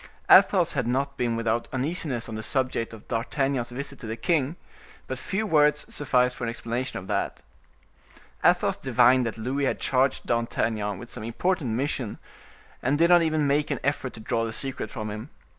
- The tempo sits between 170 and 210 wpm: Yes, average, 185 wpm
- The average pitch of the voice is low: Yes, low, 125 Hz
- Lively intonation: No, average, 3.5 semitones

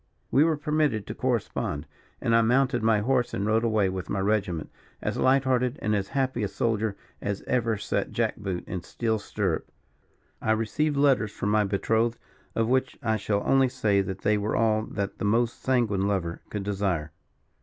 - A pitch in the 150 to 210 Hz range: No, low, 110 Hz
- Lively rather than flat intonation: No, average, 3.6 semitones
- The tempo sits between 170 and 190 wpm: Yes, average, 185 wpm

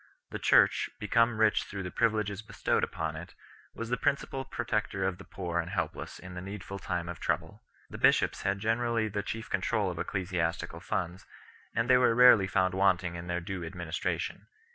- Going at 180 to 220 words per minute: Yes, average, 185 wpm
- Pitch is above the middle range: No, very low, 95 Hz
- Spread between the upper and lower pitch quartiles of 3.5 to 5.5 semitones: Yes, average, 4.0 semitones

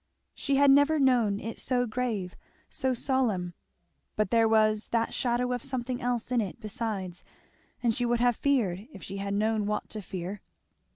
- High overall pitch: Yes, high, 230 Hz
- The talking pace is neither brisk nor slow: Yes, average, 175 wpm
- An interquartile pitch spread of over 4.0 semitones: No, average, 3.3 semitones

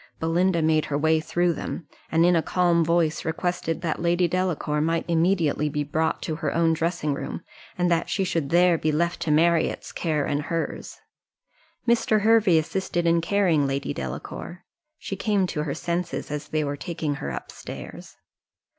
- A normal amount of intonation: No, narrow, 2.3 semitones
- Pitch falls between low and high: Yes, medium, 165 Hz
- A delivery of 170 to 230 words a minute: Yes, average, 175 wpm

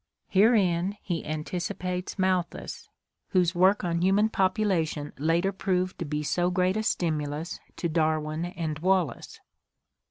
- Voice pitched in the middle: Yes, medium, 175 Hz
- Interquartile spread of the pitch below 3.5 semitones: Yes, average, 2.9 semitones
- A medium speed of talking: No, slow, 125 wpm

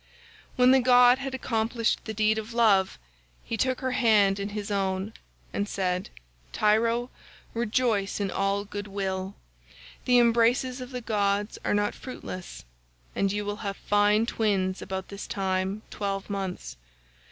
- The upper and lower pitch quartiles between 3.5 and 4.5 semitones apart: No, average, 3.0 semitones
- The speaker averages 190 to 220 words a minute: No, average, 150 wpm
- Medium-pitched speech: No, high, 210 Hz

